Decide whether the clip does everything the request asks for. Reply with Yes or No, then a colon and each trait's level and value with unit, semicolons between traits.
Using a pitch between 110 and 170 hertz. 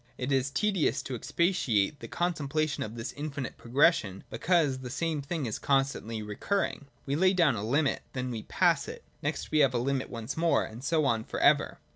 Yes: medium, 140 Hz